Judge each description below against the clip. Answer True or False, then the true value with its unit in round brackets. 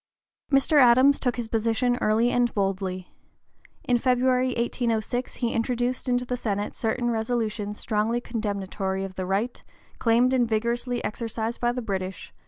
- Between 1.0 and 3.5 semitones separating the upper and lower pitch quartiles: True (2.6 semitones)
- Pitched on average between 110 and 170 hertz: False (235 Hz)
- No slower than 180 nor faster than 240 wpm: False (150 wpm)